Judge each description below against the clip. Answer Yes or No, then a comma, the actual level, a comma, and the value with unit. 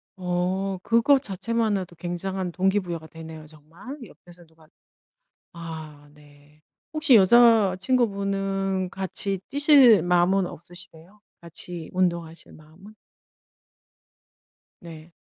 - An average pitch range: Yes, average, 3.2 semitones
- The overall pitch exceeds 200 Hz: No, medium, 185 Hz